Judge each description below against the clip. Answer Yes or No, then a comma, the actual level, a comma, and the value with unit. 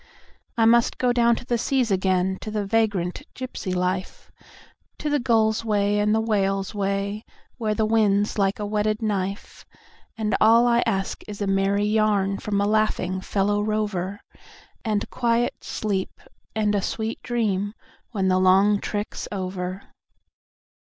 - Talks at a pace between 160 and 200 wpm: No, average, 150 wpm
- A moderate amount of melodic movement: No, narrow, 2.2 semitones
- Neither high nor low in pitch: No, high, 210 Hz